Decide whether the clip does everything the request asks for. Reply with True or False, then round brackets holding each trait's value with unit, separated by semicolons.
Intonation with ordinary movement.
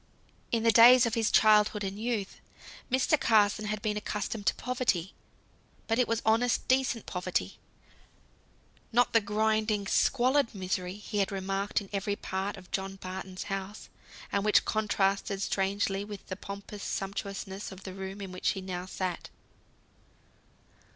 False (2.2 semitones)